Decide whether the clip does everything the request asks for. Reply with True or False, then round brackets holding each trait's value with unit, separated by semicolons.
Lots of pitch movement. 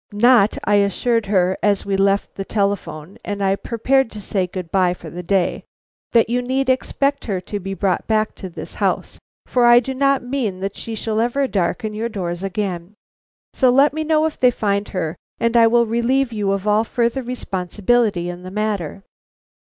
False (3.9 semitones)